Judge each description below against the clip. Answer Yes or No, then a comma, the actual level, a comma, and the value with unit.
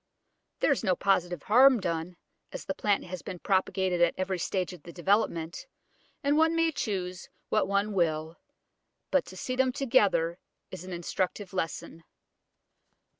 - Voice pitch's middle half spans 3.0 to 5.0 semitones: Yes, average, 3.5 semitones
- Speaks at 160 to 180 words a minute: No, average, 150 wpm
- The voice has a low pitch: No, medium, 185 Hz